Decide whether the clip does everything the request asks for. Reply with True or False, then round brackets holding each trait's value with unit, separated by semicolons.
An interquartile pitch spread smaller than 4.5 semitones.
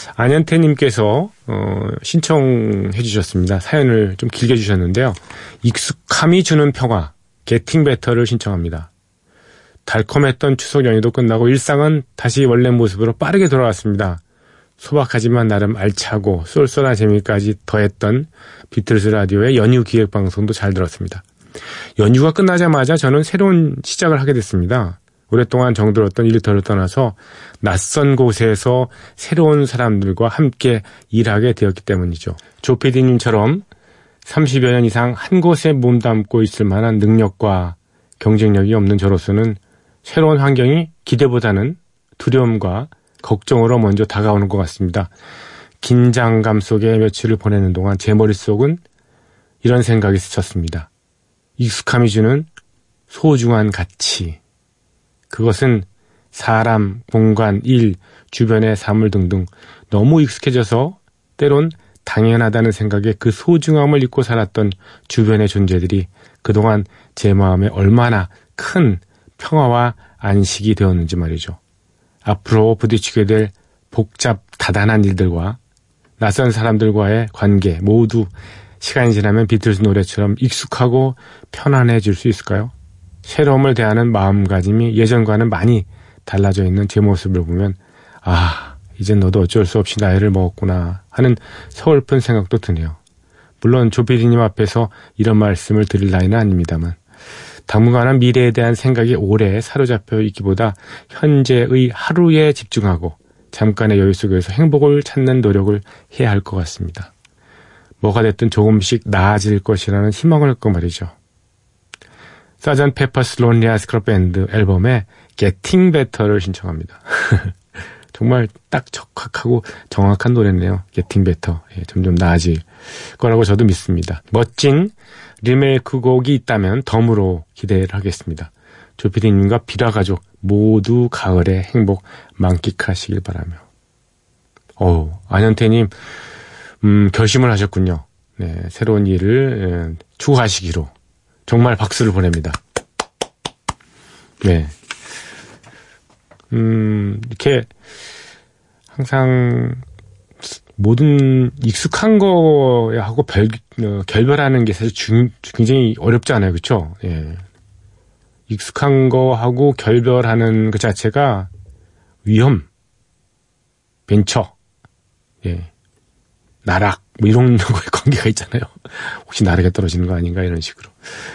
True (3.9 semitones)